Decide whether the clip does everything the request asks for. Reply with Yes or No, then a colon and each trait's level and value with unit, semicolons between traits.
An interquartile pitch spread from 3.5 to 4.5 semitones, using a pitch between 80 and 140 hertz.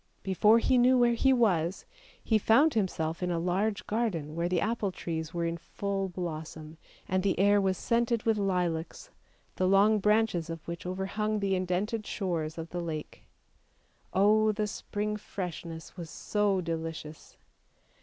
No: average, 4.1 semitones; high, 190 Hz